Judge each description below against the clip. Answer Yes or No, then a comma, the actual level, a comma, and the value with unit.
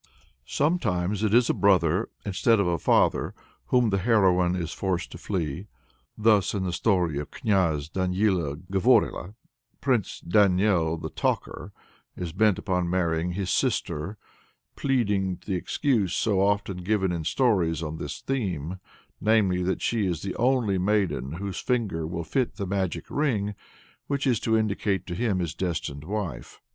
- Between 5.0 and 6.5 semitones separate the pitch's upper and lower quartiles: No, average, 3.5 semitones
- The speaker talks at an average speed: Yes, average, 155 wpm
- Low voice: Yes, very low, 95 Hz